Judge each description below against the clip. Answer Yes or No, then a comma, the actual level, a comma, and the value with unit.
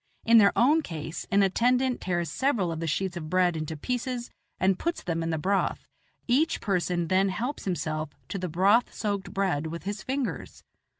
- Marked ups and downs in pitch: Yes, wide, 5.9 semitones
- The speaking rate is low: No, average, 185 wpm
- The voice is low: No, high, 190 Hz